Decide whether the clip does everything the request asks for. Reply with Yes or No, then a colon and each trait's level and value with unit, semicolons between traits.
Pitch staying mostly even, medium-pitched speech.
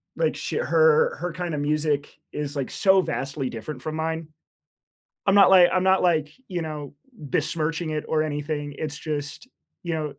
No: average, 3.4 semitones; medium, 155 Hz